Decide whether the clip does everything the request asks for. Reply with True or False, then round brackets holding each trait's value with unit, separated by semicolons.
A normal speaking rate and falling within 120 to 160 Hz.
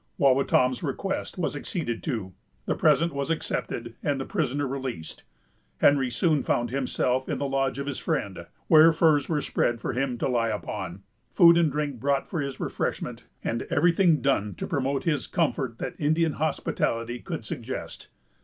True (170 wpm; 140 Hz)